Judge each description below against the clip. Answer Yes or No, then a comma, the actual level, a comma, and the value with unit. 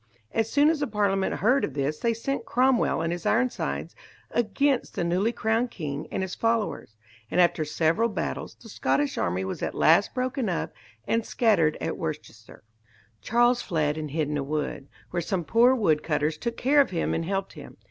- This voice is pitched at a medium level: No, high, 195 Hz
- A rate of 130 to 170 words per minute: No, average, 190 wpm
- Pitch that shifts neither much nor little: No, wide, 7.3 semitones